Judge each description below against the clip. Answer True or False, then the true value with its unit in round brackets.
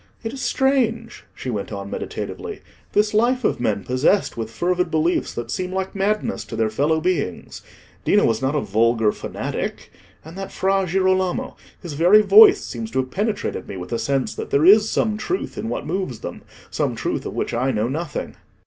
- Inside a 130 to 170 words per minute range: False (190 wpm)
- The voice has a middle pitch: True (175 Hz)